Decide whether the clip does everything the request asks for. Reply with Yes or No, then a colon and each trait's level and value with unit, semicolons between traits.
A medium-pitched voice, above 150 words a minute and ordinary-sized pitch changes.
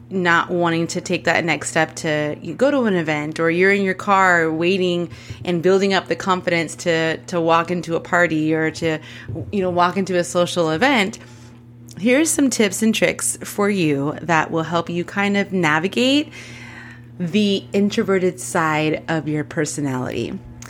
Yes: medium, 170 Hz; average, 170 wpm; average, 3.6 semitones